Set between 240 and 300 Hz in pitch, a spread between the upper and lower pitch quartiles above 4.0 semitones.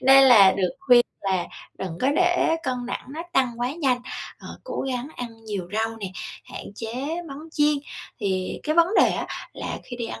Yes: high, 245 Hz; average, 4.6 semitones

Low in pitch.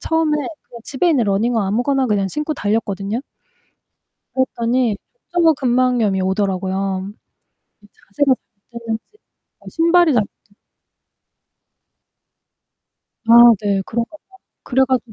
No: high, 235 Hz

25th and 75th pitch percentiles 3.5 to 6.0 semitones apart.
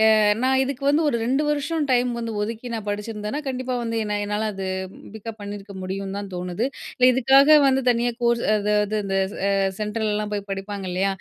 Yes: average, 3.8 semitones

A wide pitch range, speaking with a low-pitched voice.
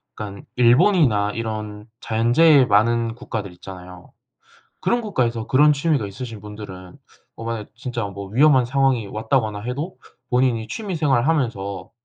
No: average, 4.3 semitones; low, 115 Hz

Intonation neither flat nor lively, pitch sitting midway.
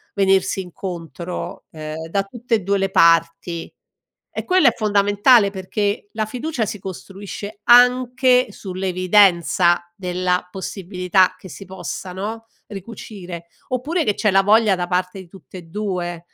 No: average, 3.0 semitones; high, 195 Hz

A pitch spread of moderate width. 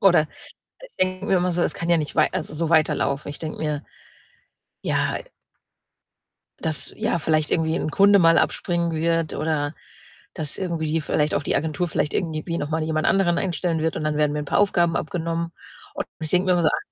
No: narrow, 2.0 semitones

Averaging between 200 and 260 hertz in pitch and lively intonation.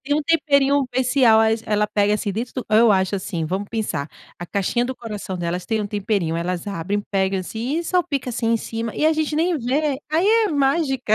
Yes: high, 225 Hz; wide, 5.9 semitones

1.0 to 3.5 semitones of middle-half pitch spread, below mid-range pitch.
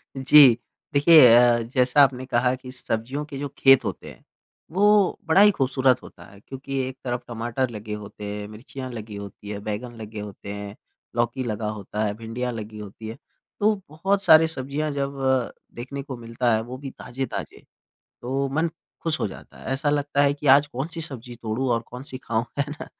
No: average, 3.9 semitones; low, 130 Hz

